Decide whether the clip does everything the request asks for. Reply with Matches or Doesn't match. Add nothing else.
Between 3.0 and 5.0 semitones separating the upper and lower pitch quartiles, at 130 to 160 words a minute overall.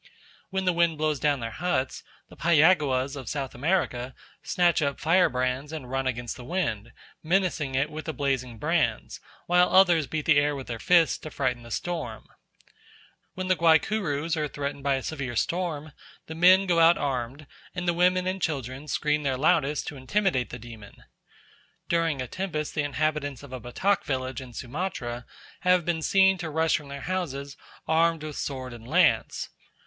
Doesn't match